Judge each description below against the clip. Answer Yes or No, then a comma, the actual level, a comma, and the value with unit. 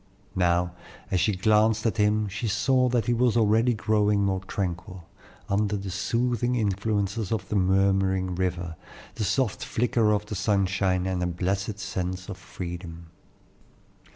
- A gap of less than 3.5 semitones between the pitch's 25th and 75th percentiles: Yes, average, 2.8 semitones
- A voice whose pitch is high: No, low, 100 Hz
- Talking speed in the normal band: Yes, average, 150 wpm